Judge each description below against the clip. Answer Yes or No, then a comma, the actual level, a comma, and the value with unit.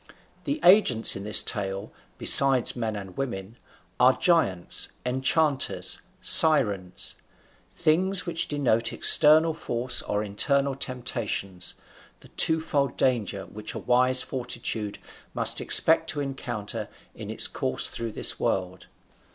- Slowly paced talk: Yes, slow, 120 wpm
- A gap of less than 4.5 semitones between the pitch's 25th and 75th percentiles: No, wide, 5.6 semitones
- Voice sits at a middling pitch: No, low, 125 Hz